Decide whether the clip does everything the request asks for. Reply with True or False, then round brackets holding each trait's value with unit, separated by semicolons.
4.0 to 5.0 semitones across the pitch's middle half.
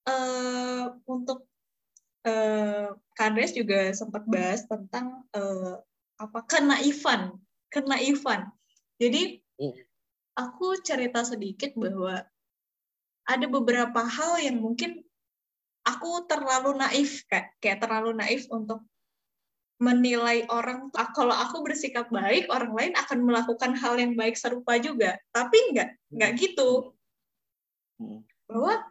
False (3.4 semitones)